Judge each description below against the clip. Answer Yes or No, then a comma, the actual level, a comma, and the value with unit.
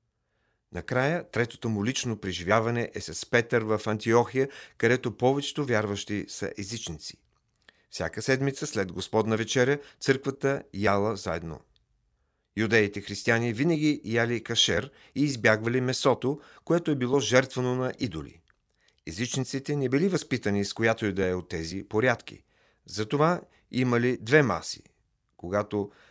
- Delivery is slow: No, average, 125 wpm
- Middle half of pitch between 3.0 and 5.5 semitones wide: Yes, average, 3.9 semitones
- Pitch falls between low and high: No, low, 115 Hz